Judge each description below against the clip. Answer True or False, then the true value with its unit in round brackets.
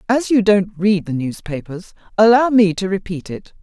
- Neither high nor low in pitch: False (195 Hz)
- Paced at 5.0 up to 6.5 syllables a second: False (4.8 syllables/s)